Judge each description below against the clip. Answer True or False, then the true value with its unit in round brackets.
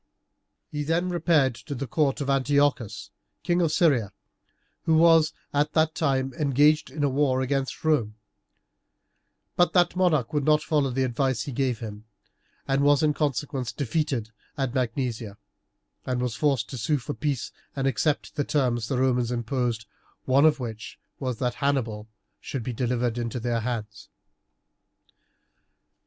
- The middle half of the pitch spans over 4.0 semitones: False (3.7 semitones)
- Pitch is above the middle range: False (135 Hz)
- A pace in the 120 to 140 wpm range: False (155 wpm)